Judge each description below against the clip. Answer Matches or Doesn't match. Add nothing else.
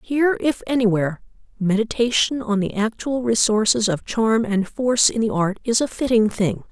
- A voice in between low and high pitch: Doesn't match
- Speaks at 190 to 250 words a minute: Doesn't match